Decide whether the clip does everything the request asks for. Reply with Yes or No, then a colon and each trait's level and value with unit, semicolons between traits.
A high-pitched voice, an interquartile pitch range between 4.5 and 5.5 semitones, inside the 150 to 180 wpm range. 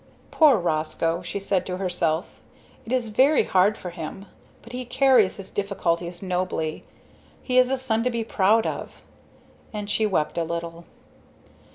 Yes: high, 195 Hz; average, 5.1 semitones; average, 160 wpm